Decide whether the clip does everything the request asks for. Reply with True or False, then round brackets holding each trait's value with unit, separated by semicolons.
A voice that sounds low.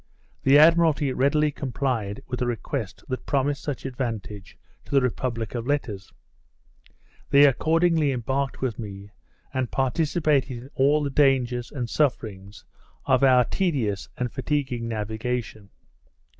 True (130 Hz)